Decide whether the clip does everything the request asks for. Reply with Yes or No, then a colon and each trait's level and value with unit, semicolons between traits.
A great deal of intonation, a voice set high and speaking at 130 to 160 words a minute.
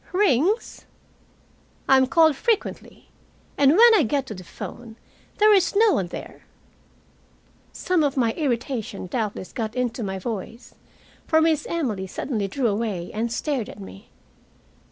Yes: wide, 6.8 semitones; very high, 250 Hz; average, 145 wpm